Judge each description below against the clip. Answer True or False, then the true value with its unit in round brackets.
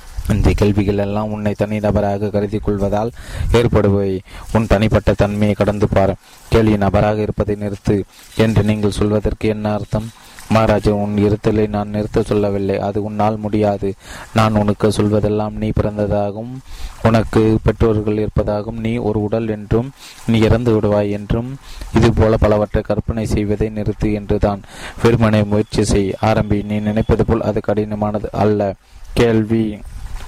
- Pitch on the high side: False (105 Hz)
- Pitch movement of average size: False (1.1 semitones)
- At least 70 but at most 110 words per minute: False (130 wpm)